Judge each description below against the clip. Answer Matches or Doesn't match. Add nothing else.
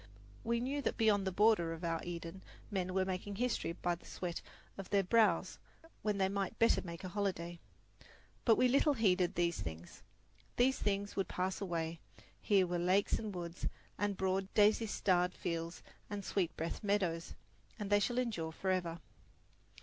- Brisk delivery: Doesn't match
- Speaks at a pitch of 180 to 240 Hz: Matches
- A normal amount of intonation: Matches